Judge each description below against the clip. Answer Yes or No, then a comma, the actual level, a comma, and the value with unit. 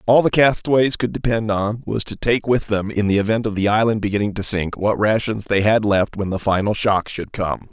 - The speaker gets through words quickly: Yes, fast, 240 wpm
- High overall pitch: No, low, 105 Hz